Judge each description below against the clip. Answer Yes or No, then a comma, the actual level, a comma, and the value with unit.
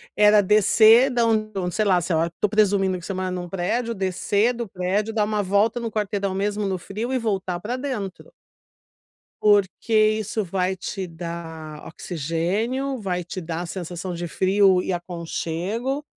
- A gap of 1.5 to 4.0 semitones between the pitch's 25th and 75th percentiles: Yes, average, 3.3 semitones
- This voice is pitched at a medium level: No, high, 195 Hz